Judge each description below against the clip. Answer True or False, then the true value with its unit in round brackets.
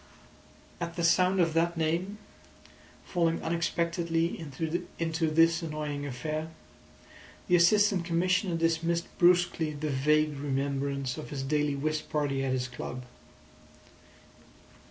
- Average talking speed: False (115 wpm)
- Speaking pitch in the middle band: True (160 Hz)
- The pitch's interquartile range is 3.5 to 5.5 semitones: False (2.7 semitones)